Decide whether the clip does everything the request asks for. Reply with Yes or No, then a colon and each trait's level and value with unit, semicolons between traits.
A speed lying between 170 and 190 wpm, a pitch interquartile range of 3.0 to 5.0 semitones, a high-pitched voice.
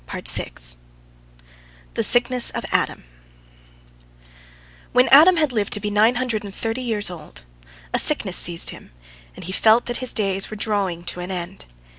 No: average, 155 wpm; average, 4.5 semitones; high, 210 Hz